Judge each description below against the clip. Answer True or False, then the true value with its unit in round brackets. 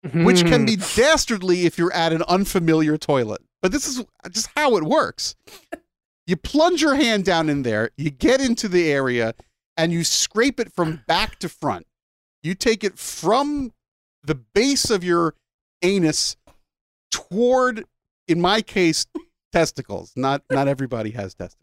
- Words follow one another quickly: False (155 wpm)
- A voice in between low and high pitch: True (175 Hz)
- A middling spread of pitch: False (6.7 semitones)